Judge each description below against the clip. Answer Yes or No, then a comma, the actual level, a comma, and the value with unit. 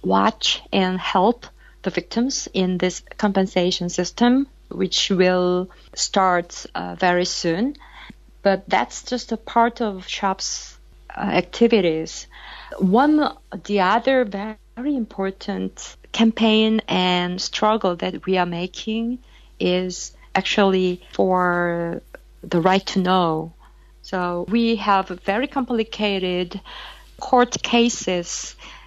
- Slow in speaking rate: Yes, slow, 105 wpm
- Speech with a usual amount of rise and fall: Yes, average, 4.0 semitones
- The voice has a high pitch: Yes, high, 195 Hz